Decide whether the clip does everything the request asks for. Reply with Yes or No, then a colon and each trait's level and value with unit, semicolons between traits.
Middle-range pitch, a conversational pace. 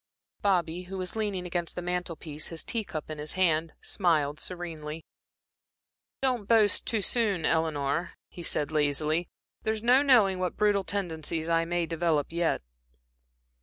Yes: medium, 175 Hz; average, 150 wpm